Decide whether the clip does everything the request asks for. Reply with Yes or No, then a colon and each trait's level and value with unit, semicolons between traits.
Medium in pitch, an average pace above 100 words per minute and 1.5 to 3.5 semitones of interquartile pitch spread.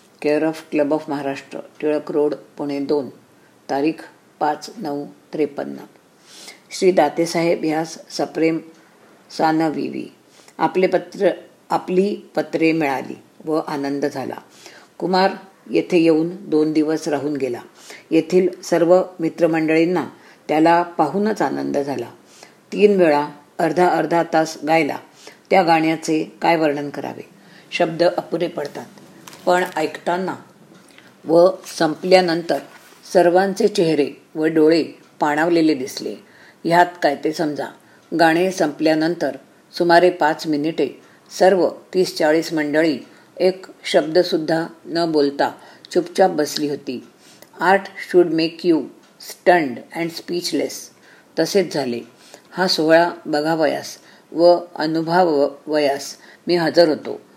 Yes: medium, 160 Hz; average, 110 wpm; narrow, 2.4 semitones